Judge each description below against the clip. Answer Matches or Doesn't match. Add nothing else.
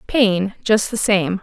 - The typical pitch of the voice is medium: Doesn't match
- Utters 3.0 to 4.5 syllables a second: Matches